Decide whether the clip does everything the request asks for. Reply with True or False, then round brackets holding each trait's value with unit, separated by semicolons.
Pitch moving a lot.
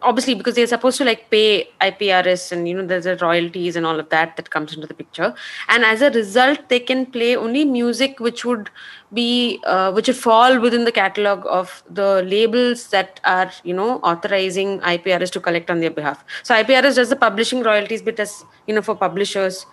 False (4.7 semitones)